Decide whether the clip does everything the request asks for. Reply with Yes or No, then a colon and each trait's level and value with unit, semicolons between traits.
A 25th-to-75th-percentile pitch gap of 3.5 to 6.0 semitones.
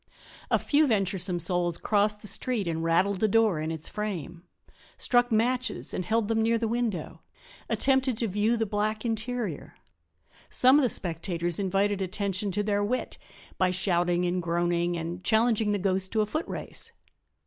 Yes: average, 4.2 semitones